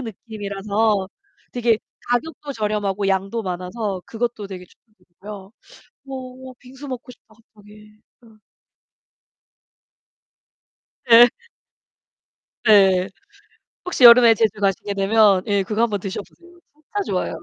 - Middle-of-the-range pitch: No, high, 215 Hz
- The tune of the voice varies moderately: Yes, average, 3.4 semitones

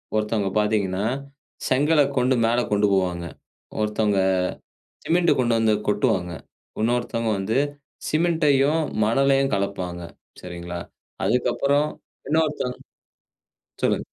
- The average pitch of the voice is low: Yes, low, 115 Hz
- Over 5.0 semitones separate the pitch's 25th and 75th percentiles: Yes, wide, 5.5 semitones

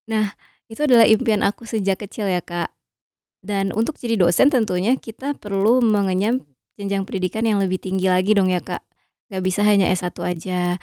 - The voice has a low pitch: No, high, 200 Hz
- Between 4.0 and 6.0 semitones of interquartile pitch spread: No, average, 3.0 semitones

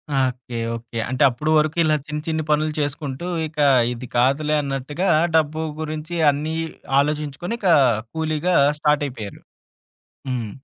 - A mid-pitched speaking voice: Yes, medium, 150 Hz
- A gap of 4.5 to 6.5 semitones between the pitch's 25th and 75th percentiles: No, average, 3.1 semitones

